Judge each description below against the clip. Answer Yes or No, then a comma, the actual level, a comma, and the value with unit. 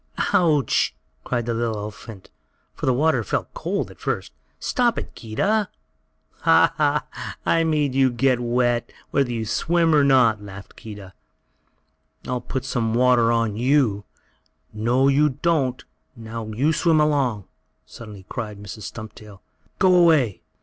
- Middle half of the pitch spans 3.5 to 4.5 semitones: No, average, 4.9 semitones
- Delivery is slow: No, average, 145 wpm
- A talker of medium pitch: No, low, 125 Hz